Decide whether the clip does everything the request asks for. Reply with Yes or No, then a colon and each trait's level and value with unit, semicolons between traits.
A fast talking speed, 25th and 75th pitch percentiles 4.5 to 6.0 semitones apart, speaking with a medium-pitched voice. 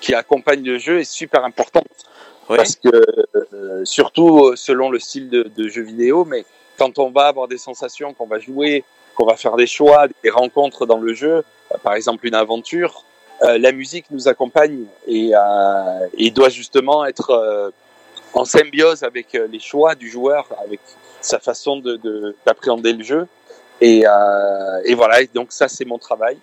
No: fast, 180 wpm; average, 5.1 semitones; low, 130 Hz